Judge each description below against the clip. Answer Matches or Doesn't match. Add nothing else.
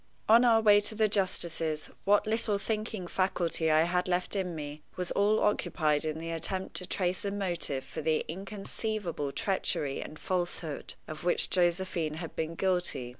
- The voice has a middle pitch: Matches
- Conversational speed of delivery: Matches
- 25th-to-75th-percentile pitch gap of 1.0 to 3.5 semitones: Doesn't match